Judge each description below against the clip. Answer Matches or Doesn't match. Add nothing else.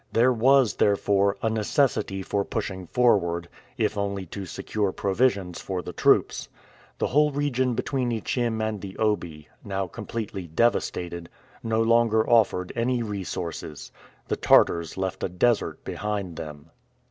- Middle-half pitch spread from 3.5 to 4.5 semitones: Matches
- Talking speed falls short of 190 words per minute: Matches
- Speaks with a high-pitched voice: Doesn't match